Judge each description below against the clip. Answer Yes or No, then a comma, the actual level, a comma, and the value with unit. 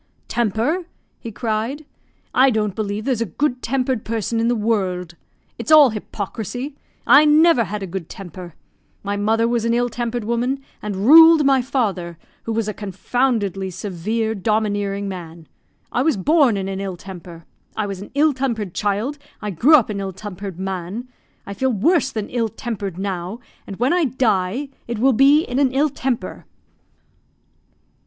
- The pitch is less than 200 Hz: No, high, 220 Hz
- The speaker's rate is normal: Yes, average, 170 wpm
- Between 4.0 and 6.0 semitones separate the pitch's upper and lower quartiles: Yes, average, 4.7 semitones